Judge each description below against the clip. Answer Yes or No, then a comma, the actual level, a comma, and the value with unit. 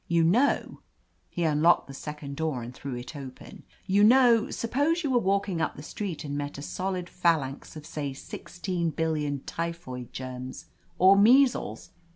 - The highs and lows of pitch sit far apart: Yes, wide, 5.7 semitones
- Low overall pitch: No, medium, 165 Hz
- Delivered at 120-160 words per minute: No, average, 170 wpm